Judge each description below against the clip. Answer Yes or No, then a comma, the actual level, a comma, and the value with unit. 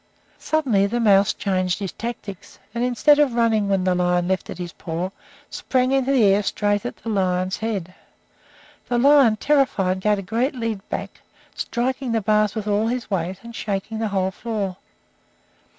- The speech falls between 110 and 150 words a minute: No, average, 170 wpm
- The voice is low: No, high, 210 Hz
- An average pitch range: Yes, average, 3.9 semitones